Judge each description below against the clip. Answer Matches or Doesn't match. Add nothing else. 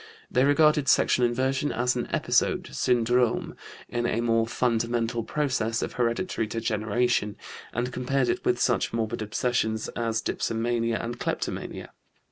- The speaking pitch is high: Doesn't match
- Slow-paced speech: Matches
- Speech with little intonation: Matches